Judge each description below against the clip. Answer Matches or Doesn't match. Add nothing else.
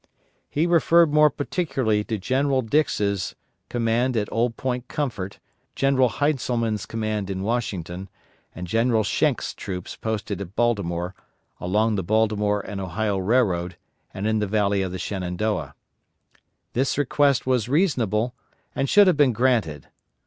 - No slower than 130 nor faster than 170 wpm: Matches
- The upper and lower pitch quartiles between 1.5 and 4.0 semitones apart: Doesn't match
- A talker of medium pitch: Doesn't match